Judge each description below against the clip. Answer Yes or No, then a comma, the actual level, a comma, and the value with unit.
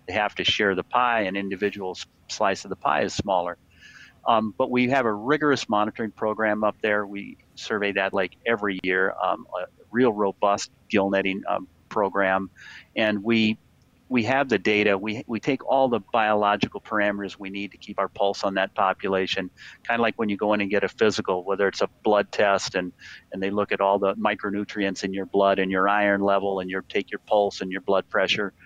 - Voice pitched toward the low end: Yes, low, 100 Hz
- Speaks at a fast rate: Yes, fast, 210 wpm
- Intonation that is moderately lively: No, narrow, 1.6 semitones